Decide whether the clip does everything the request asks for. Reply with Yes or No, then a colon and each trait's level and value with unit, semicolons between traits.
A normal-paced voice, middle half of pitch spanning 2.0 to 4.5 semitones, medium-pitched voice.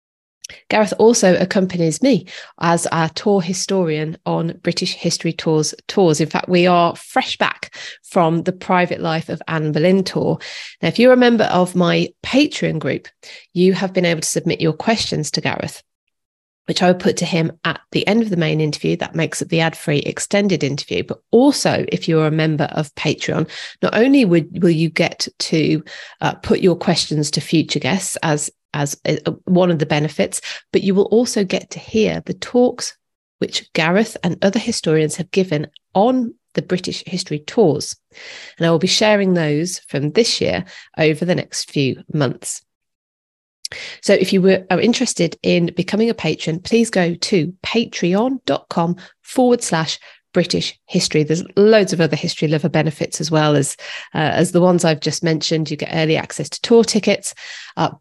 Yes: average, 180 wpm; average, 3.6 semitones; medium, 175 Hz